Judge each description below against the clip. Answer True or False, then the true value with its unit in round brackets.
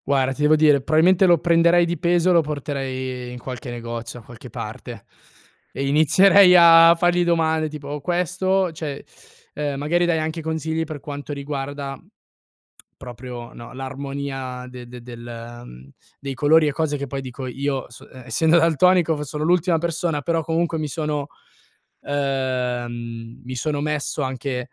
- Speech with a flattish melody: False (3.9 semitones)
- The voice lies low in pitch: False (145 Hz)